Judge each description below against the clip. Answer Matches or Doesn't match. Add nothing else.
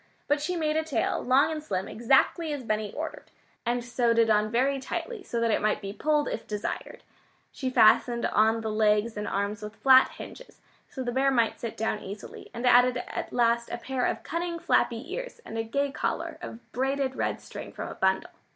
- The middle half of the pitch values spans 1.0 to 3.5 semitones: Doesn't match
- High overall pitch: Matches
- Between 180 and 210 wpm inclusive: Matches